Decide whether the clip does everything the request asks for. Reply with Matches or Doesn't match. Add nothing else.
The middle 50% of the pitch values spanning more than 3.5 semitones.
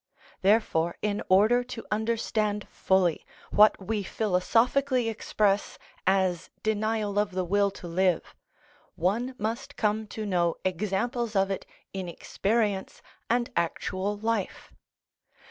Doesn't match